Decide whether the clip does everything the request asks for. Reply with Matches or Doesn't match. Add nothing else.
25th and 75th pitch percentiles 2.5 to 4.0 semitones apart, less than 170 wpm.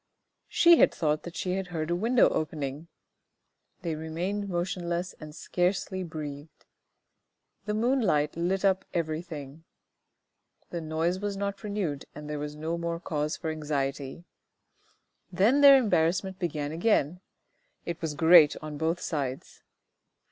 Matches